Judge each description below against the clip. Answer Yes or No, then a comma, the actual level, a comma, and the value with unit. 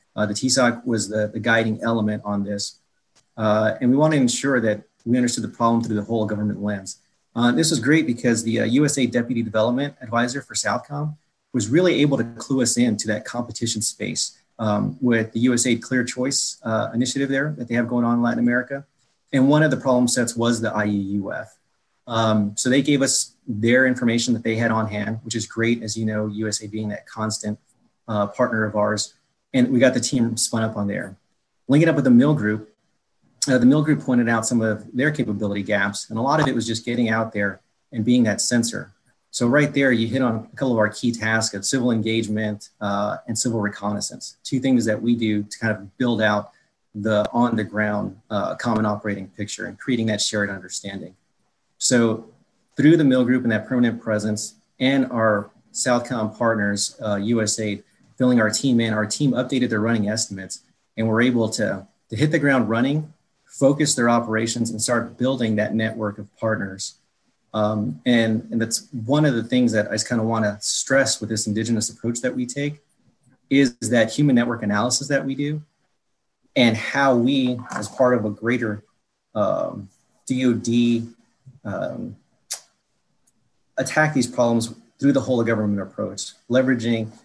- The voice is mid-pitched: No, low, 115 Hz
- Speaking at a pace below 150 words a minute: No, average, 195 wpm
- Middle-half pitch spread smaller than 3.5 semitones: Yes, average, 2.7 semitones